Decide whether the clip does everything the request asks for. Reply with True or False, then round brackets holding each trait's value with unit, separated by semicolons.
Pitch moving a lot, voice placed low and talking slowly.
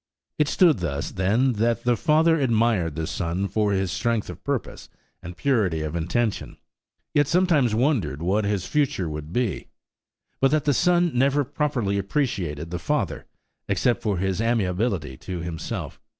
False (7.3 semitones; 105 Hz; 155 wpm)